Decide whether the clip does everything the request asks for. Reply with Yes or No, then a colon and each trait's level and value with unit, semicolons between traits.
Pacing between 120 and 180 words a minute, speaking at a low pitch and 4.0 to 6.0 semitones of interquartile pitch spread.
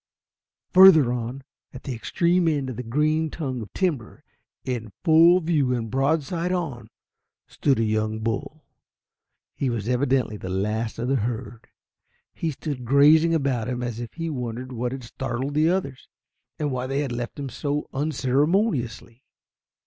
Yes: average, 155 wpm; low, 130 Hz; average, 4.4 semitones